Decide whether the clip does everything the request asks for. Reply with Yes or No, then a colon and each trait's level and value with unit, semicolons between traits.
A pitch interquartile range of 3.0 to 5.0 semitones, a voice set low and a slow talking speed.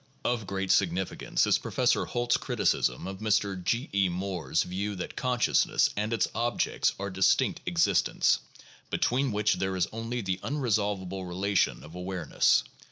No: average, 3.5 semitones; low, 100 Hz; average, 145 wpm